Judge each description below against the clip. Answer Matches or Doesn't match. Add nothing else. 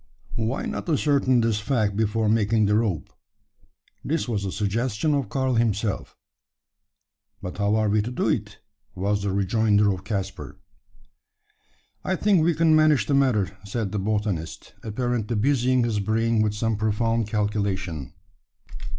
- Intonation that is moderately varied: Matches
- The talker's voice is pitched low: Matches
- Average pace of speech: Matches